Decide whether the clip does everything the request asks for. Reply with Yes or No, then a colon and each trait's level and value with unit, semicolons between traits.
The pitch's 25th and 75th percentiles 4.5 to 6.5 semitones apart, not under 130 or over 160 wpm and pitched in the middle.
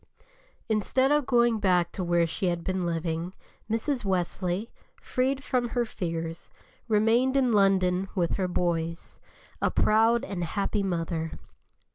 No: average, 5.2 semitones; slow, 135 wpm; high, 195 Hz